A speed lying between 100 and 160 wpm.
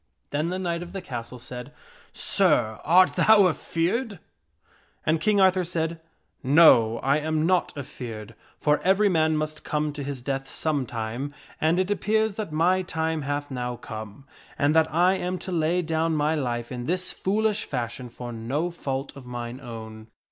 No: average, 180 wpm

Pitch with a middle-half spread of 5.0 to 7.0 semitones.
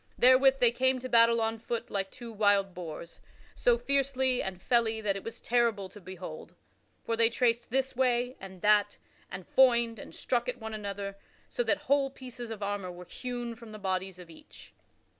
No: average, 3.9 semitones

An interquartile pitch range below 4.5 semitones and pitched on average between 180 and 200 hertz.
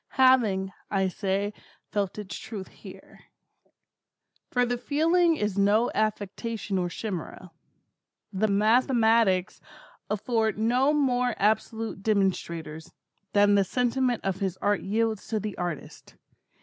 No: average, 3.6 semitones; high, 215 Hz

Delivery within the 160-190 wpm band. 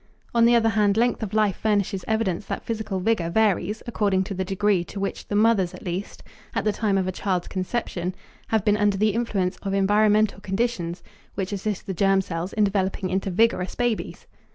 No: average, 200 wpm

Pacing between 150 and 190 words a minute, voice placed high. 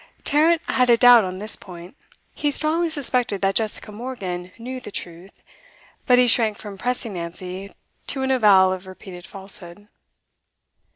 Yes: average, 155 wpm; high, 210 Hz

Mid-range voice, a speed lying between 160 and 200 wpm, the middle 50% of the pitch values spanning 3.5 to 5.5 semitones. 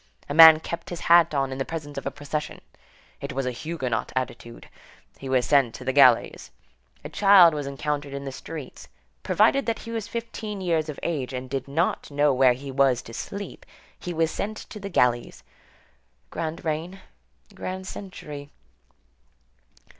Yes: medium, 150 Hz; average, 170 wpm; average, 4.3 semitones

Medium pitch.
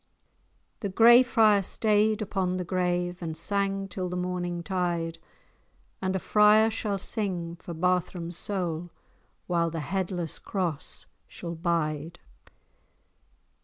Yes: medium, 180 Hz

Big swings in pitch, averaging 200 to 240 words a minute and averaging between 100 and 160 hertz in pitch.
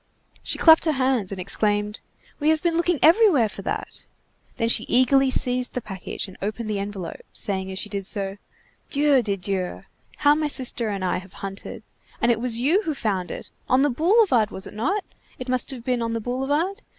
No: wide, 6.1 semitones; fast, 205 wpm; high, 240 Hz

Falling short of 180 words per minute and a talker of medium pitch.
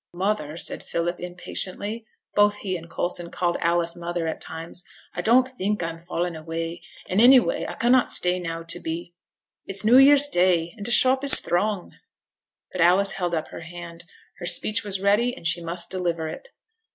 No: average, 190 wpm; medium, 180 Hz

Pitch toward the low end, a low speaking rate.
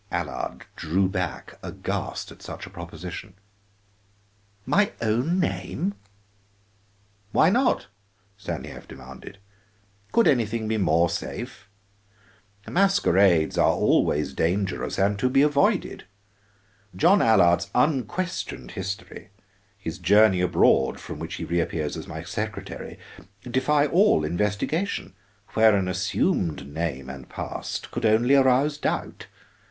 Yes: low, 100 Hz; slow, 115 wpm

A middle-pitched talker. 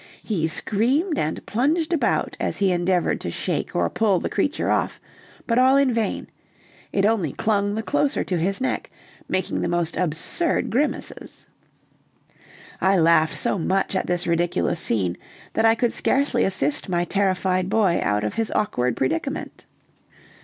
No: high, 195 Hz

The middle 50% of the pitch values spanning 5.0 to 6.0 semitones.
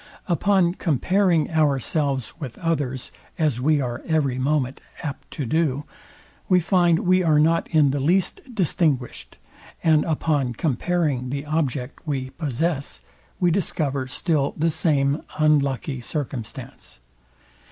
No: average, 3.7 semitones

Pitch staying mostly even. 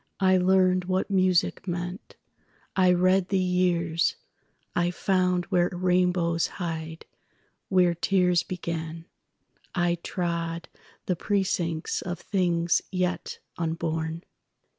Yes: narrow, 1.5 semitones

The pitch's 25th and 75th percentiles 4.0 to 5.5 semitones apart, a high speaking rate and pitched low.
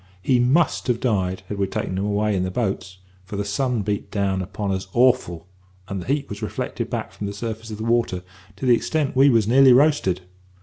Yes: average, 4.4 semitones; fast, 220 wpm; low, 105 Hz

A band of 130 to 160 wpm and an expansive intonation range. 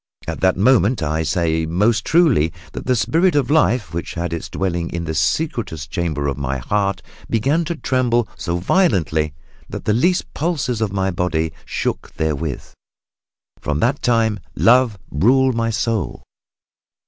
Yes: average, 155 wpm; wide, 7.6 semitones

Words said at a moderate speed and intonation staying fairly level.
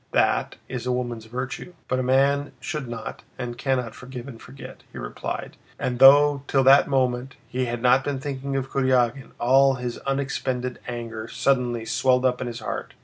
Yes: average, 180 wpm; narrow, 1.9 semitones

